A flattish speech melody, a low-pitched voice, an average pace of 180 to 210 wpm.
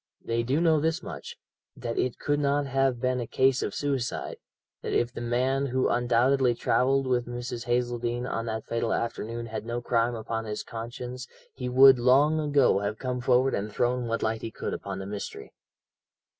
Yes: narrow, 2.2 semitones; low, 120 Hz; average, 185 wpm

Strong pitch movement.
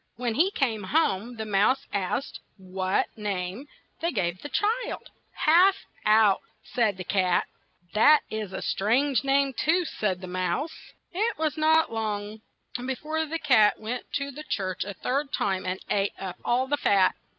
Yes: wide, 6.9 semitones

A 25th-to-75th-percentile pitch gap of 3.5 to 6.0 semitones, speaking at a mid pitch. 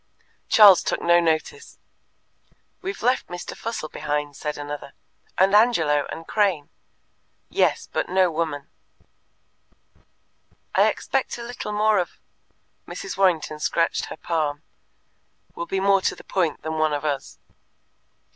Yes: average, 4.8 semitones; medium, 170 Hz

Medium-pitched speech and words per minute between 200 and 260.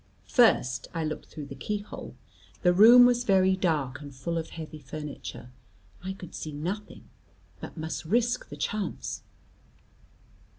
No: medium, 170 Hz; average, 145 wpm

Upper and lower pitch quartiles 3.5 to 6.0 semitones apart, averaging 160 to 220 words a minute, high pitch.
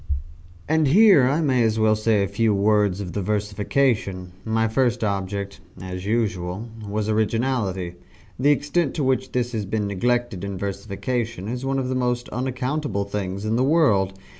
No: average, 4.2 semitones; average, 165 wpm; low, 110 Hz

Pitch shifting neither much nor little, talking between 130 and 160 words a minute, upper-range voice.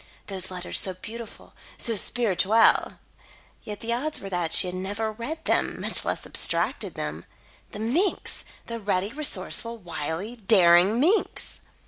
Yes: average, 4.1 semitones; average, 140 wpm; high, 210 Hz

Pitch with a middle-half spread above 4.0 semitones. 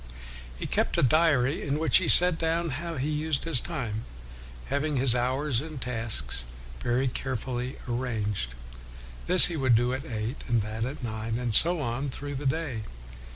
Yes: average, 4.4 semitones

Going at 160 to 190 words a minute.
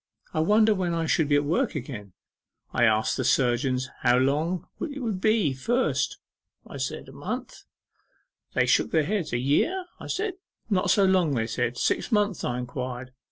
Yes: average, 180 wpm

